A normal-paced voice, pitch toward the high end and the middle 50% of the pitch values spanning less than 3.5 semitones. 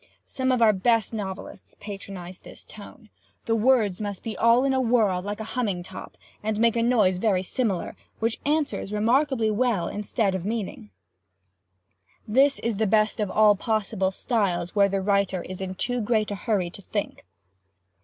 Yes: average, 175 wpm; high, 215 Hz; average, 3.1 semitones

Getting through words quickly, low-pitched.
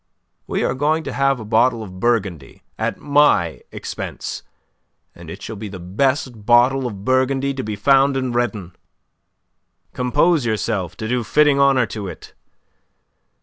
No: average, 150 wpm; low, 120 Hz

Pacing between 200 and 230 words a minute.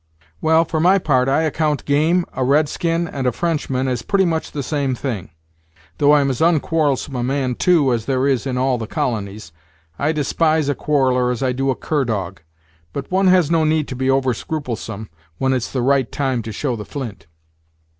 Yes: fast, 205 wpm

